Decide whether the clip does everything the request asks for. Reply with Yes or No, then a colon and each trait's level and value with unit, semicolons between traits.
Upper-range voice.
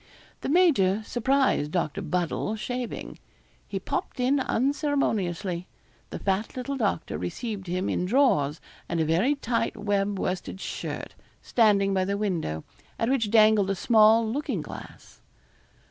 Yes: high, 210 Hz